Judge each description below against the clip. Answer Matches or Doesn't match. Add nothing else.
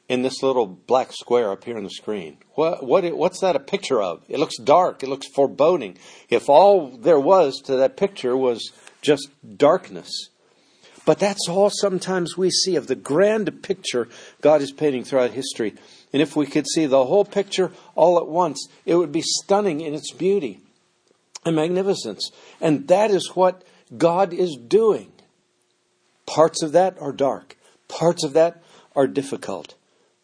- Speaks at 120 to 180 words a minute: Matches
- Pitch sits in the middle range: Matches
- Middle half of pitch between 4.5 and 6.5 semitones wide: Matches